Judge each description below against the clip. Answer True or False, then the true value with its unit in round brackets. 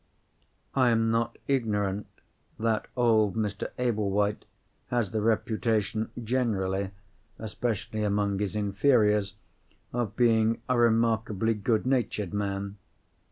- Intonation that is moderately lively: False (2.2 semitones)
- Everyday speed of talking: False (105 wpm)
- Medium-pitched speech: False (110 Hz)